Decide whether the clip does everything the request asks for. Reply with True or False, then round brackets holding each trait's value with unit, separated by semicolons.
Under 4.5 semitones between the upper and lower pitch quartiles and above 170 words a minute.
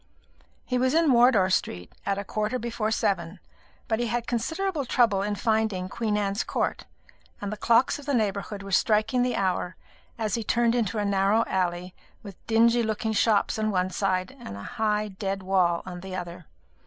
True (3.4 semitones; 185 wpm)